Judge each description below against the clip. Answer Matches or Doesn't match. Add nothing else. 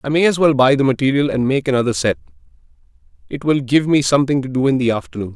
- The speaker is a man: Matches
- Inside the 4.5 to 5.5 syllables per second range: Doesn't match